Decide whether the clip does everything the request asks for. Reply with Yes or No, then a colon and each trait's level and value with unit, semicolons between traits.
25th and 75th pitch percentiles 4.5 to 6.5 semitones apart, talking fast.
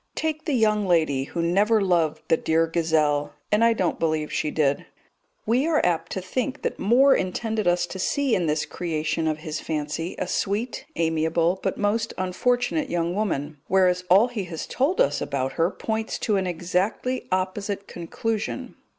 No: average, 5.2 semitones; average, 175 wpm